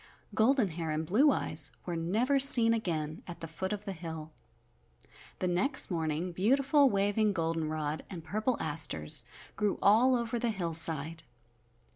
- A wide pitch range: Yes, wide, 5.8 semitones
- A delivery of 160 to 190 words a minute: No, average, 150 wpm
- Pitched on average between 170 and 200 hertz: Yes, medium, 185 Hz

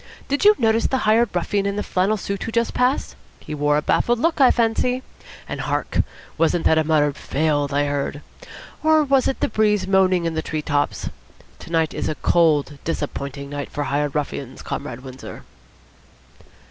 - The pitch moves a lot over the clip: Yes, wide, 7.4 semitones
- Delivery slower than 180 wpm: No, average, 185 wpm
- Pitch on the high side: No, medium, 165 Hz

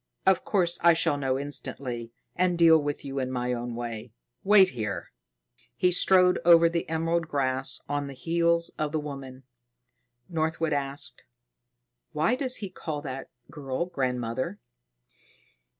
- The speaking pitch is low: No, medium, 150 Hz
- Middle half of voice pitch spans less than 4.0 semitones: No, average, 4.5 semitones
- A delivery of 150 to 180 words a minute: No, average, 140 wpm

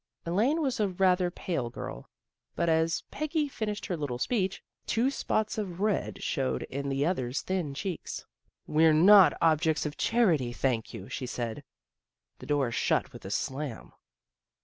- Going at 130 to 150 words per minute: No, average, 160 wpm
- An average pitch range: No, wide, 6.8 semitones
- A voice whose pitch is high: No, medium, 165 Hz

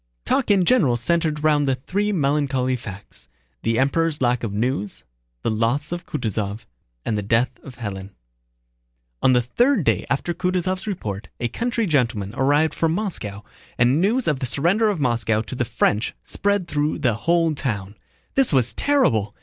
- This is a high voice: No, low, 135 Hz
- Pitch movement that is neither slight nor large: No, wide, 7.0 semitones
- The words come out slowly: No, average, 165 wpm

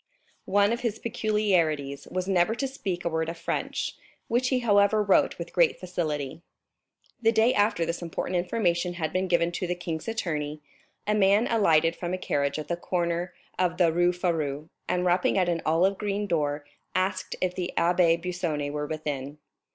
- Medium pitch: Yes, medium, 175 Hz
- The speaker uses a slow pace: No, average, 180 wpm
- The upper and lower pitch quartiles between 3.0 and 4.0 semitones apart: Yes, average, 3.6 semitones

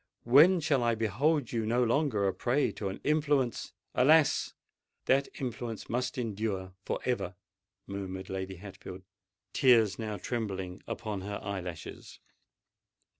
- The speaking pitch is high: No, low, 115 Hz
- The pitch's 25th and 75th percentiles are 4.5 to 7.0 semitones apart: Yes, average, 4.9 semitones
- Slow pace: Yes, slow, 130 wpm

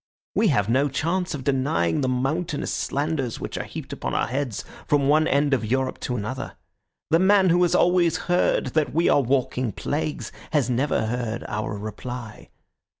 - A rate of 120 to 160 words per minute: No, average, 175 wpm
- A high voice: No, low, 135 Hz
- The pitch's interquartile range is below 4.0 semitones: No, average, 4.3 semitones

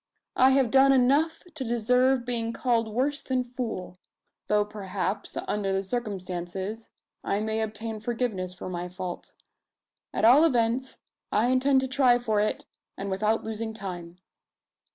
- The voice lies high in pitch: Yes, high, 225 Hz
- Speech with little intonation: No, average, 4.1 semitones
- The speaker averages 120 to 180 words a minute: Yes, average, 145 wpm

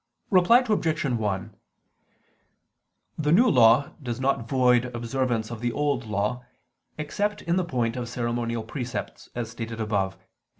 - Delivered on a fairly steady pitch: No, average, 4.0 semitones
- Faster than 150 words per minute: No, average, 140 wpm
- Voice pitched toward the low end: Yes, low, 120 Hz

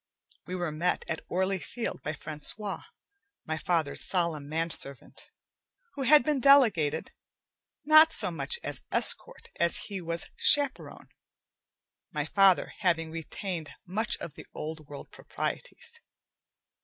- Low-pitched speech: No, medium, 175 Hz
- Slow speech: Yes, slow, 125 wpm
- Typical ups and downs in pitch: No, wide, 7.1 semitones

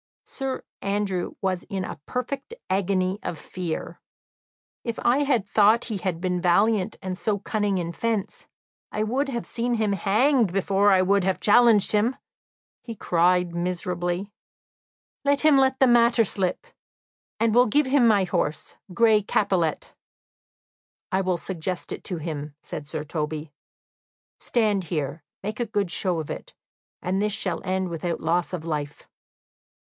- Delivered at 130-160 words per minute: Yes, average, 150 wpm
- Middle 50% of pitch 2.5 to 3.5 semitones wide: No, average, 4.2 semitones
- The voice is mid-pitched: No, high, 195 Hz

